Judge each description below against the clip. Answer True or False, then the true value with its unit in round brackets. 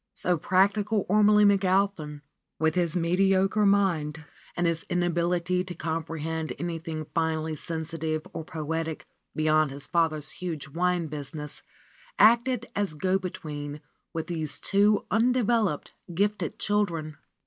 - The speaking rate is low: True (120 wpm)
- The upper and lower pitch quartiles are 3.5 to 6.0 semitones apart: True (3.8 semitones)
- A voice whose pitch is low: False (170 Hz)